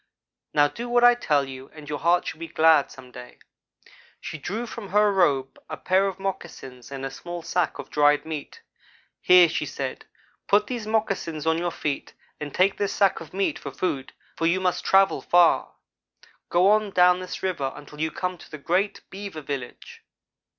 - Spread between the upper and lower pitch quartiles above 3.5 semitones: Yes, average, 4.8 semitones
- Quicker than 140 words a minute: Yes, average, 190 wpm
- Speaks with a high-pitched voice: No, medium, 175 Hz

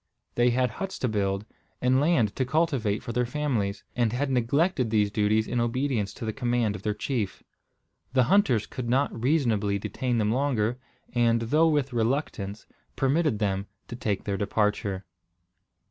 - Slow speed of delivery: No, average, 160 wpm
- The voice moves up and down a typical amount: Yes, average, 4.0 semitones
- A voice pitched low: Yes, low, 120 Hz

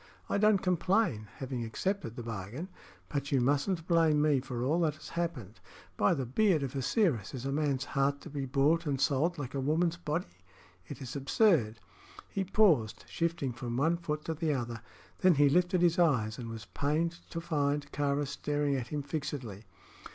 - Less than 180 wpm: No, average, 185 wpm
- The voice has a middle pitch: Yes, medium, 145 Hz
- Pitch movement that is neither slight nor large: Yes, average, 4.6 semitones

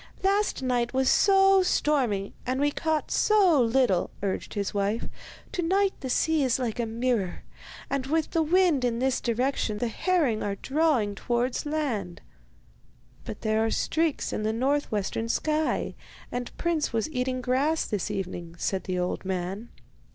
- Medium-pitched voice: No, very high, 255 Hz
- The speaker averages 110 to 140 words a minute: No, average, 160 wpm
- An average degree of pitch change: No, wide, 6.1 semitones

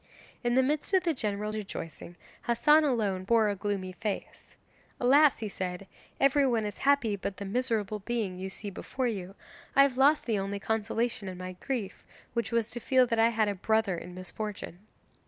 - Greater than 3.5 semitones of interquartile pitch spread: Yes, average, 3.9 semitones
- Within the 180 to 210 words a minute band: Yes, average, 185 wpm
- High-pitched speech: Yes, high, 220 Hz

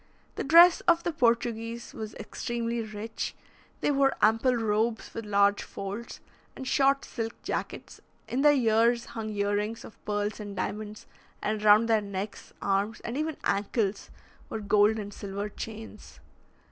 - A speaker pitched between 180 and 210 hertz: No, high, 220 Hz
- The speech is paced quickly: No, average, 150 wpm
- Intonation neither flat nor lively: No, narrow, 2.3 semitones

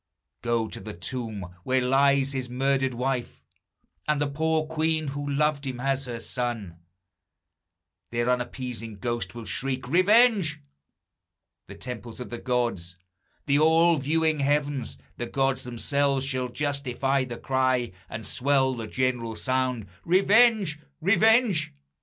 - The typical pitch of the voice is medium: No, low, 130 Hz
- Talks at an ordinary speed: No, slow, 130 wpm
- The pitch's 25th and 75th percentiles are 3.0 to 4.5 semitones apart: Yes, average, 3.5 semitones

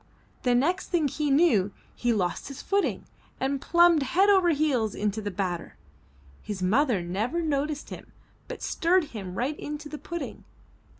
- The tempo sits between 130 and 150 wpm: No, average, 160 wpm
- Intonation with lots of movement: Yes, wide, 7.6 semitones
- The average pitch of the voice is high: Yes, very high, 280 Hz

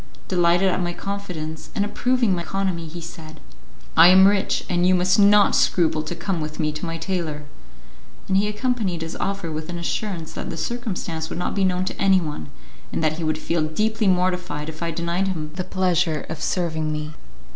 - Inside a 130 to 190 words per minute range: No, average, 200 wpm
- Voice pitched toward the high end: No, medium, 175 Hz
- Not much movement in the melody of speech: No, average, 3.2 semitones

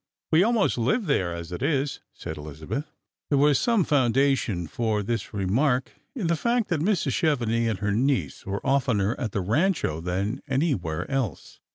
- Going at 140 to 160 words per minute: No, average, 170 wpm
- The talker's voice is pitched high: No, low, 125 Hz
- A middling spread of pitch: No, wide, 7.1 semitones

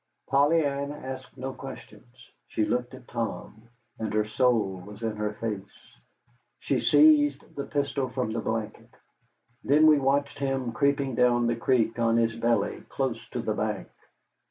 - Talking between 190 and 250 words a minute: No, average, 155 wpm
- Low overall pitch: Yes, low, 125 Hz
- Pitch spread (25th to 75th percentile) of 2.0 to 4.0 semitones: Yes, average, 3.6 semitones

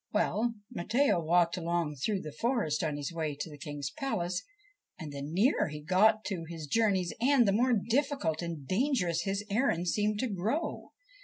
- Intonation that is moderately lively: No, wide, 5.8 semitones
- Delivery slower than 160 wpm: No, average, 175 wpm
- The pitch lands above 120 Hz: Yes, medium, 185 Hz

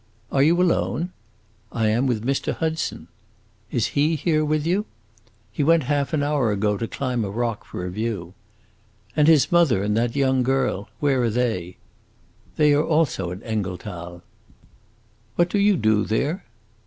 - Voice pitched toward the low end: Yes, low, 130 Hz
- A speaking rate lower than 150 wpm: No, average, 165 wpm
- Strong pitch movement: Yes, wide, 6.1 semitones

